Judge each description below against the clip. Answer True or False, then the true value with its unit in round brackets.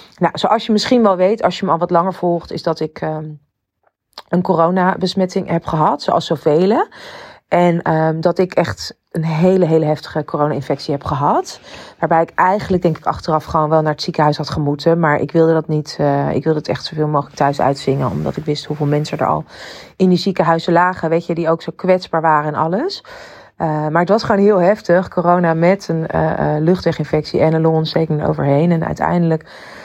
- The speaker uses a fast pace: True (205 wpm)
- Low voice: False (165 Hz)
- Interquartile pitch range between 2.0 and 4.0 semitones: True (2.8 semitones)